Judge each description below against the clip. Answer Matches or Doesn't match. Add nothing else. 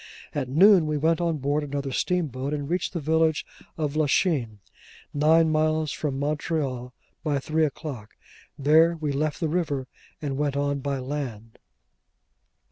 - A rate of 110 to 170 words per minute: Matches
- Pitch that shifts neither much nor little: Doesn't match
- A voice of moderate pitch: Matches